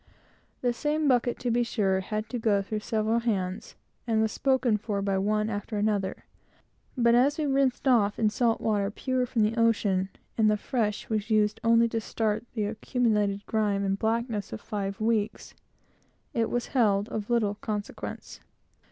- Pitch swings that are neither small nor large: No, narrow, 2.3 semitones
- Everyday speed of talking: Yes, average, 170 wpm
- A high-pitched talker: Yes, high, 220 Hz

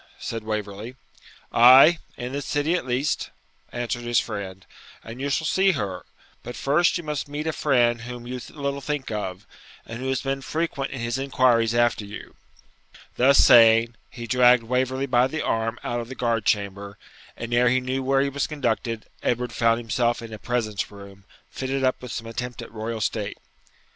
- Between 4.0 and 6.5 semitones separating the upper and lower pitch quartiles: No, average, 2.8 semitones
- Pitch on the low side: Yes, low, 120 Hz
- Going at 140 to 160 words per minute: No, average, 185 wpm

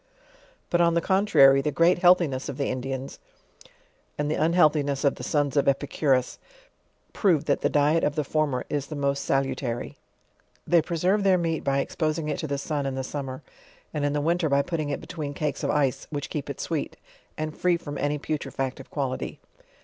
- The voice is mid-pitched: Yes, medium, 145 Hz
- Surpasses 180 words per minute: Yes, average, 200 wpm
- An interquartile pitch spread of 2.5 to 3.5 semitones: Yes, average, 2.8 semitones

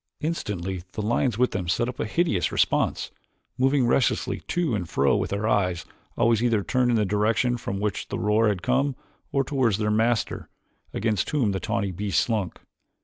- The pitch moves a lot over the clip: No, average, 3.8 semitones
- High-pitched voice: No, low, 110 Hz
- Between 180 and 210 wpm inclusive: Yes, average, 185 wpm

